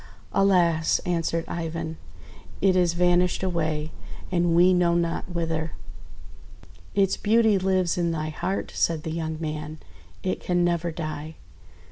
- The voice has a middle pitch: Yes, medium, 170 Hz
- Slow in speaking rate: Yes, slow, 130 wpm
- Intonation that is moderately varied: No, narrow, 2.1 semitones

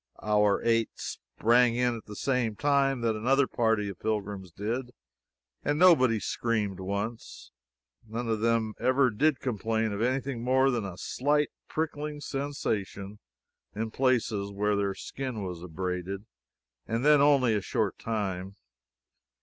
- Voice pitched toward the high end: No, low, 115 Hz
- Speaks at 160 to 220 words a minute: No, average, 145 wpm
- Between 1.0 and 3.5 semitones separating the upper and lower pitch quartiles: No, average, 4.1 semitones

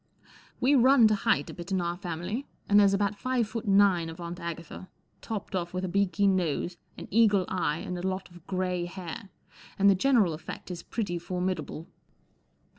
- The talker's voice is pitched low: No, medium, 185 Hz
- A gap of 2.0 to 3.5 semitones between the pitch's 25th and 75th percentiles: Yes, average, 2.8 semitones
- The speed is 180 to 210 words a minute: Yes, average, 190 wpm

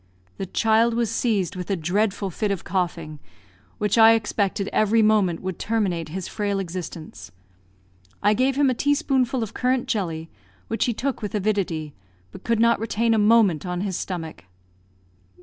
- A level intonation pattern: No, average, 4.0 semitones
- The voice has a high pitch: Yes, high, 205 Hz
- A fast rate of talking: No, average, 165 wpm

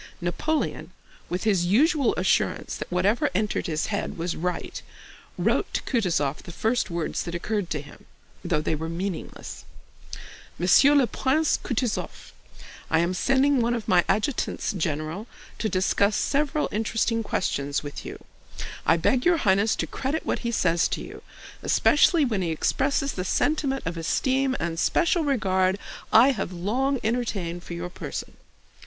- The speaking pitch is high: Yes, high, 205 Hz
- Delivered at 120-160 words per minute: Yes, average, 155 wpm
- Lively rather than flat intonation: Yes, wide, 7.2 semitones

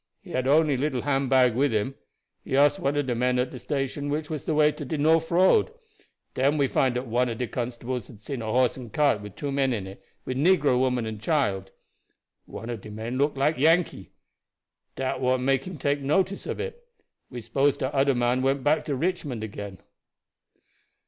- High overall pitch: No, low, 135 Hz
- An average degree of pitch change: Yes, average, 3.1 semitones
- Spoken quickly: Yes, fast, 210 wpm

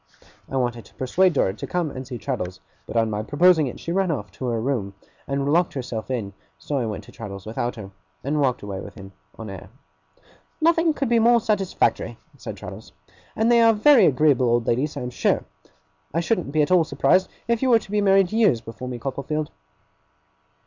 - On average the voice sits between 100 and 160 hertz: Yes, medium, 140 Hz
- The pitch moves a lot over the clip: Yes, wide, 8.5 semitones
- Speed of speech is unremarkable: No, fast, 210 wpm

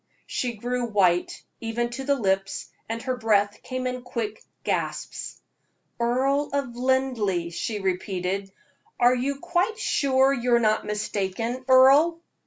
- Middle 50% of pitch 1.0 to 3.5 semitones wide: No, average, 4.0 semitones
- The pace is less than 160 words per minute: Yes, slow, 135 wpm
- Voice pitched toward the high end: Yes, high, 240 Hz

